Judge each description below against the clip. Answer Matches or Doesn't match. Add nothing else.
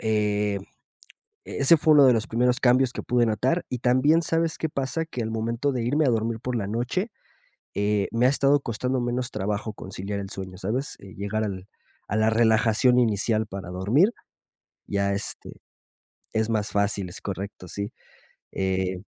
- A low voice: Matches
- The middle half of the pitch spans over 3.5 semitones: Matches